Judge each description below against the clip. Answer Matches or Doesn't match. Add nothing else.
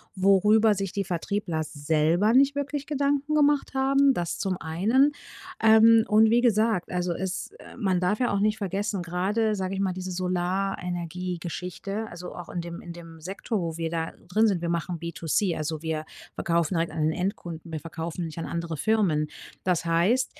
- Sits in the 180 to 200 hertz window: Matches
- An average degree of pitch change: Matches